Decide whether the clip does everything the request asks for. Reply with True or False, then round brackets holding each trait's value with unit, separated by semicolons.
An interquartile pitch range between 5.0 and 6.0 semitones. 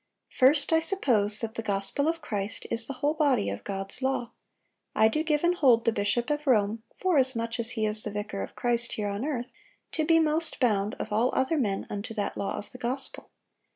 True (5.4 semitones)